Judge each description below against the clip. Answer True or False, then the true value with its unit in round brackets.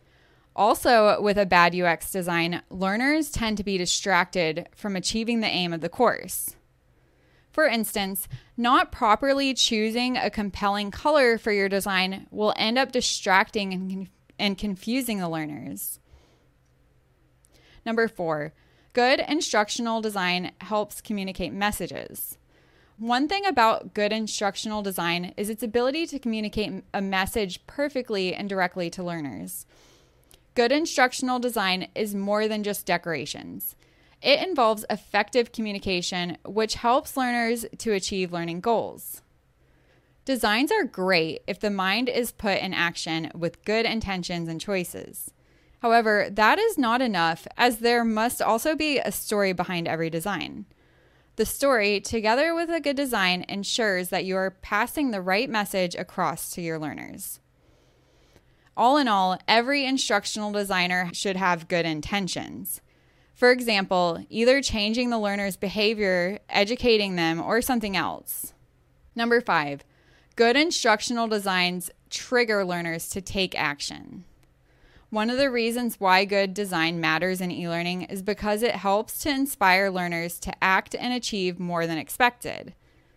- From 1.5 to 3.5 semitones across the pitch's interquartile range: False (4.5 semitones)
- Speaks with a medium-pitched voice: False (205 Hz)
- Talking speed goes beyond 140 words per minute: False (135 wpm)